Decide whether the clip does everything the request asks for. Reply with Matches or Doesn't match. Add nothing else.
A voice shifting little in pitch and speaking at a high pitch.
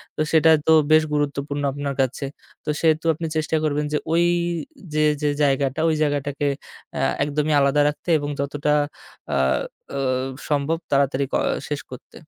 Doesn't match